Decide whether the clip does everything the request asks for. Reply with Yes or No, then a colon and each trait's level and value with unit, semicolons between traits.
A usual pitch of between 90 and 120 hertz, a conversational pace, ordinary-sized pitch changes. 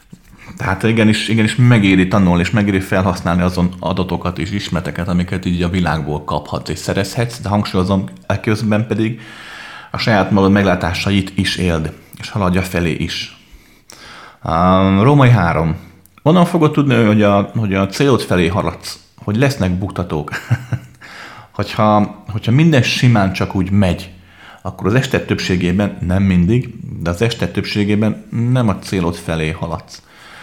Yes: very low, 95 Hz; average, 140 wpm; average, 3.4 semitones